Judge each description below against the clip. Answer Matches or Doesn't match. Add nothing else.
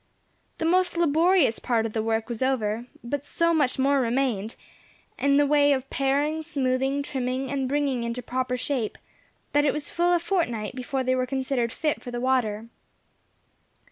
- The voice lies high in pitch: Matches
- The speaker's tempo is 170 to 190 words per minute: Matches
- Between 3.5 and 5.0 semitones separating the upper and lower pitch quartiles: Doesn't match